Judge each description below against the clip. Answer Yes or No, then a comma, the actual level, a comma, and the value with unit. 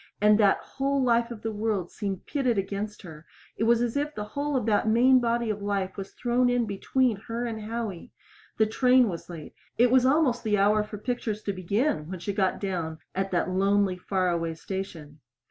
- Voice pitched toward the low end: No, high, 210 Hz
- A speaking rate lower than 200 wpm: No, fast, 205 wpm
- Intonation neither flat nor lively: Yes, average, 3.8 semitones